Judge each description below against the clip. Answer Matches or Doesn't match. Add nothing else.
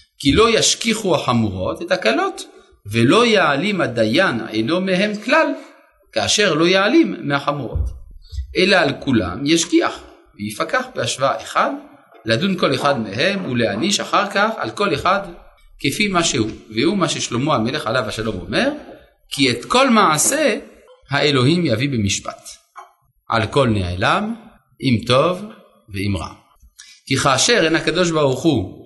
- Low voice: Doesn't match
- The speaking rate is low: Doesn't match